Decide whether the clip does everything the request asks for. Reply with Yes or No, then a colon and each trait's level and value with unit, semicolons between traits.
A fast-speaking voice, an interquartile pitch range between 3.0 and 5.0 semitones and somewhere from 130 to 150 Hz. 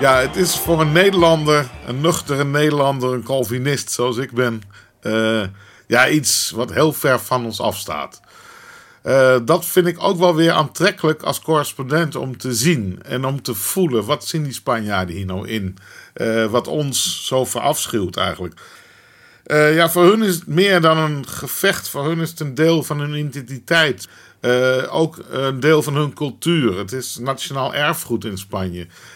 No: average, 175 wpm; average, 4.7 semitones; medium, 140 Hz